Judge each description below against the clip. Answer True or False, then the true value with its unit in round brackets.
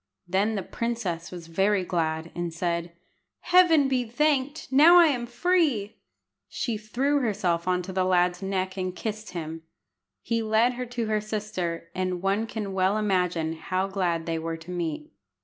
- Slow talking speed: False (165 wpm)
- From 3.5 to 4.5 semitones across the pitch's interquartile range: False (4.9 semitones)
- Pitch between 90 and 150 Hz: False (195 Hz)